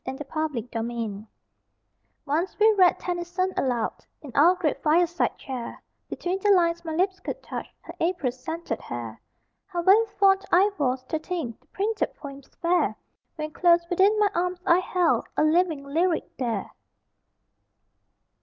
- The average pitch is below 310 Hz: No, very high, 340 Hz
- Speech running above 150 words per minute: No, average, 145 wpm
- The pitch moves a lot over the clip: No, average, 4.8 semitones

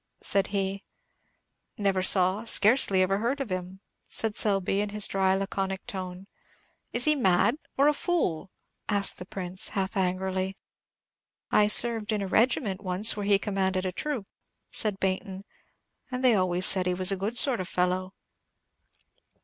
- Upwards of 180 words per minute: No, average, 155 wpm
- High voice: Yes, high, 195 Hz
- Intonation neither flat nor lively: No, narrow, 2.3 semitones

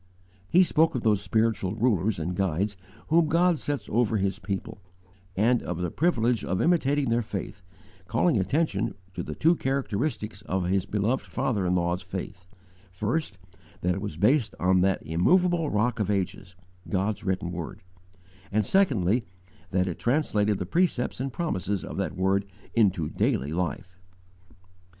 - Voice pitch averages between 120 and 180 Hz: No, low, 105 Hz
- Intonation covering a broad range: Yes, wide, 5.7 semitones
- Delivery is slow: No, average, 155 wpm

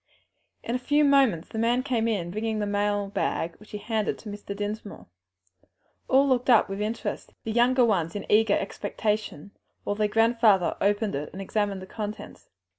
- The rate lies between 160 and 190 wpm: Yes, average, 180 wpm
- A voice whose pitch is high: Yes, high, 215 Hz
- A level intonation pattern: Yes, narrow, 2.2 semitones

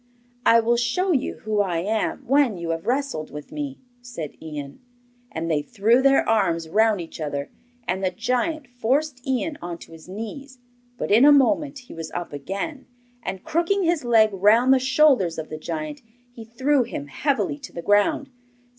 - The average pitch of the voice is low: No, high, 225 Hz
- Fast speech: No, average, 180 wpm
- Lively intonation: Yes, wide, 8.0 semitones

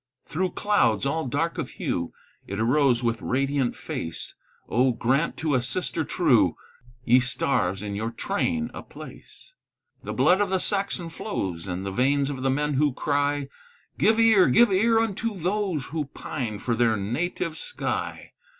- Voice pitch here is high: No, medium, 140 Hz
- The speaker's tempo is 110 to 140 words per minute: No, average, 160 wpm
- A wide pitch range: Yes, wide, 7.4 semitones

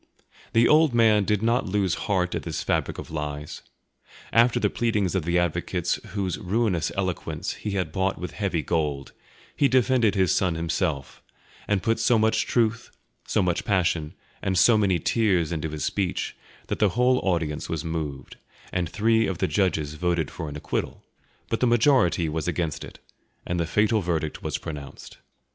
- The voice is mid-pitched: No, very low, 95 Hz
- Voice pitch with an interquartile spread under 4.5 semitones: No, average, 5.1 semitones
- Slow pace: No, average, 175 wpm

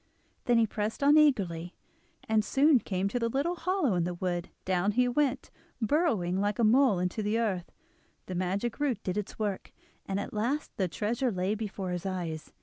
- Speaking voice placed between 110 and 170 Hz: No, high, 210 Hz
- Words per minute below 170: No, average, 190 wpm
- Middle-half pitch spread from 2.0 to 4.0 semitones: No, average, 5.1 semitones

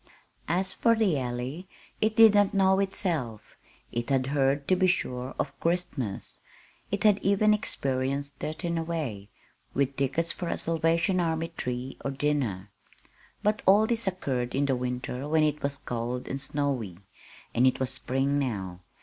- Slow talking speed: No, average, 165 wpm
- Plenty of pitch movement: Yes, wide, 6.0 semitones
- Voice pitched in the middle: Yes, medium, 145 Hz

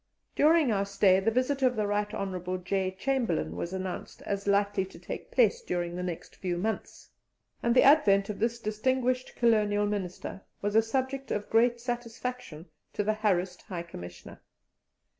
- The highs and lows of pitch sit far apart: No, average, 4.4 semitones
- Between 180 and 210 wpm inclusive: No, average, 165 wpm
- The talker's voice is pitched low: No, high, 205 Hz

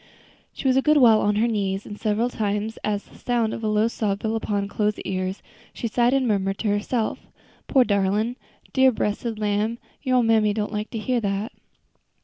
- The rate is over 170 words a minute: Yes, average, 200 wpm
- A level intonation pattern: Yes, narrow, 2.3 semitones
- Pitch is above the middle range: Yes, high, 215 Hz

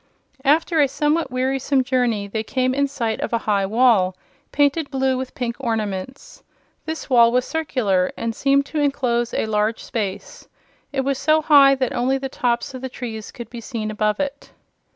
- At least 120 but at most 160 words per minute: No, average, 180 wpm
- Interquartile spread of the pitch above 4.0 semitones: No, average, 3.6 semitones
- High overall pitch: Yes, very high, 255 Hz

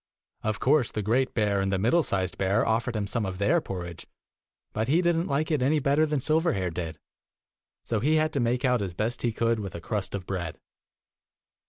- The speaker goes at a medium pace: No, fast, 215 wpm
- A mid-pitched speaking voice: No, low, 115 Hz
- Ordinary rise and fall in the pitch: No, wide, 6.3 semitones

